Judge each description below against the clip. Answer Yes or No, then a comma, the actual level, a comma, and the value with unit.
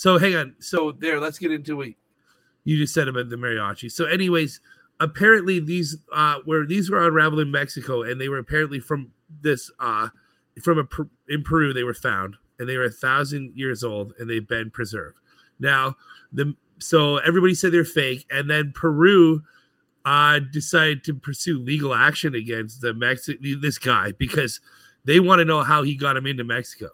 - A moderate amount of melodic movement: Yes, average, 3.8 semitones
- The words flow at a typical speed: Yes, average, 185 wpm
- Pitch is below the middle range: No, medium, 150 Hz